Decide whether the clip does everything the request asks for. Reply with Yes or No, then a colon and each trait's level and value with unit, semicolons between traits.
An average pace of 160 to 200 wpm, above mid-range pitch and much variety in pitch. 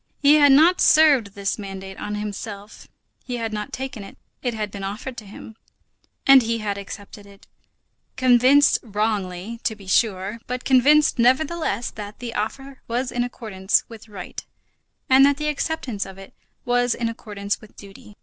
No: average, 170 wpm; high, 225 Hz; average, 4.3 semitones